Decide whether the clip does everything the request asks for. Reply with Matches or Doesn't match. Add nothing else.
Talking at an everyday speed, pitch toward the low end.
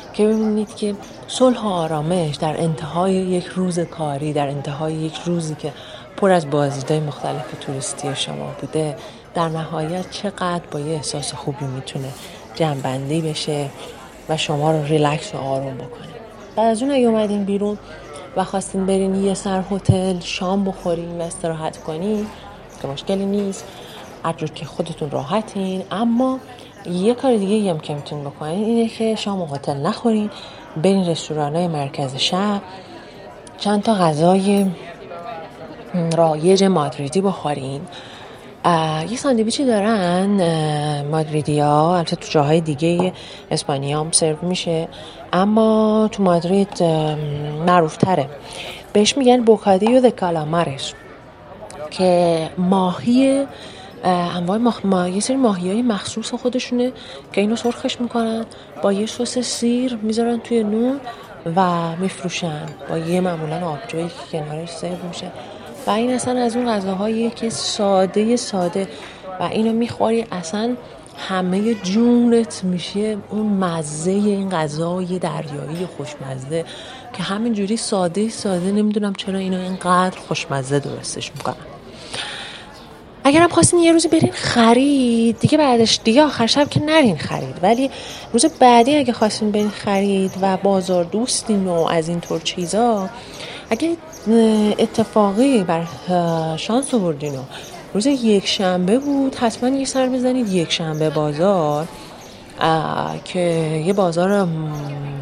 Doesn't match